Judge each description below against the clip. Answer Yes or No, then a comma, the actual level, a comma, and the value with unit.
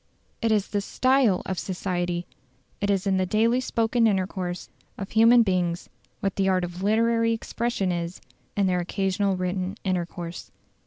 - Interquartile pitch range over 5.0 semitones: No, average, 3.5 semitones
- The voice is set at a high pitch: Yes, high, 195 Hz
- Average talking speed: Yes, average, 155 wpm